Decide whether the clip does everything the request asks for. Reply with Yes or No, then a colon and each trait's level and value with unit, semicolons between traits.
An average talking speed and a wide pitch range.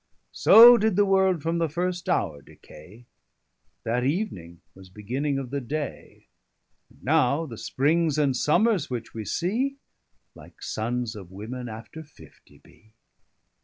Yes: average, 145 wpm; wide, 7.4 semitones